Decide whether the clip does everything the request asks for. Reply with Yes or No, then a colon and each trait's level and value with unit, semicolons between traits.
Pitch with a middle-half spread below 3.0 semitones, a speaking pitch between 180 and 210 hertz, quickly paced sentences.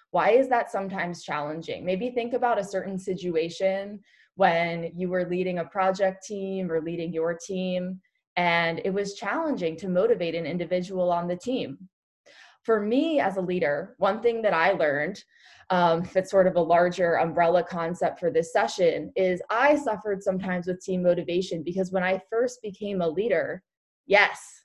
No: narrow, 2.6 semitones; medium, 185 Hz; average, 170 wpm